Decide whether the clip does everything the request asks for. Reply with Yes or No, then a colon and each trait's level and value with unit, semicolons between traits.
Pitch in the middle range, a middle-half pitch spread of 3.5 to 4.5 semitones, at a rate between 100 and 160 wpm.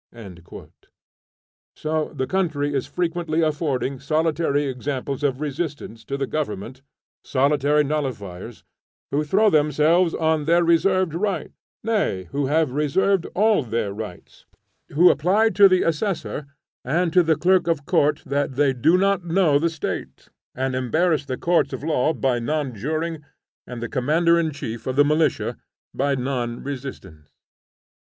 Yes: medium, 150 Hz; average, 4.0 semitones; average, 145 wpm